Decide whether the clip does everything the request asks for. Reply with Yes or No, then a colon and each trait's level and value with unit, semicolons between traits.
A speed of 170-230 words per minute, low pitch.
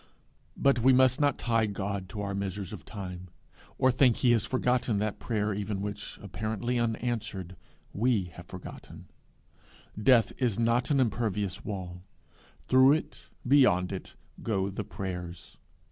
No: average, 145 wpm; low, 105 Hz